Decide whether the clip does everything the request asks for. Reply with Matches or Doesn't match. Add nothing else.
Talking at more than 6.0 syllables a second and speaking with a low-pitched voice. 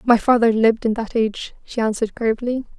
Doesn't match